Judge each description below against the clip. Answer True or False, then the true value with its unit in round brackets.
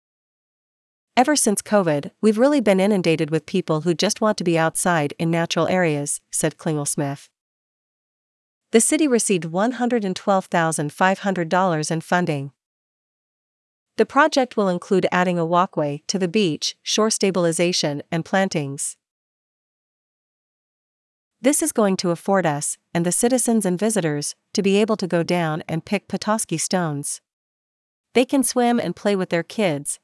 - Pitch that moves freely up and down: False (4.6 semitones)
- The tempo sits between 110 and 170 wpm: True (140 wpm)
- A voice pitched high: False (180 Hz)